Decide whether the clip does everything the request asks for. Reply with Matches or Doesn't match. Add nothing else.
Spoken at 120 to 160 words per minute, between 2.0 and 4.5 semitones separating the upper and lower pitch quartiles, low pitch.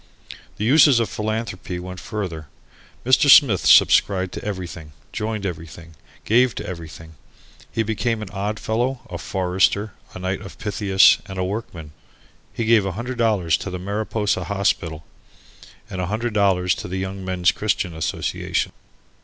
Matches